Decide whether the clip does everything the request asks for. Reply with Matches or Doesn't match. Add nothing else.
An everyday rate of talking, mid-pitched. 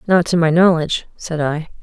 Matches